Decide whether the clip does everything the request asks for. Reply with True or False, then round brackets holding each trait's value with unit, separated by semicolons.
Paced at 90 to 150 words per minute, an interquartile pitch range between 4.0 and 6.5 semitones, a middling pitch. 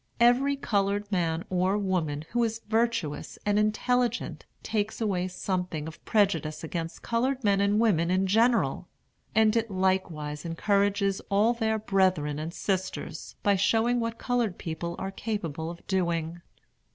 False (140 wpm; 4.4 semitones; 195 Hz)